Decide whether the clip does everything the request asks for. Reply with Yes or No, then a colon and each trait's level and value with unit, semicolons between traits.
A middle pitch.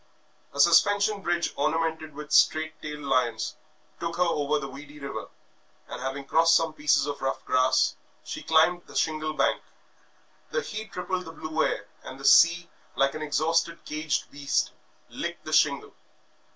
Yes: medium, 155 Hz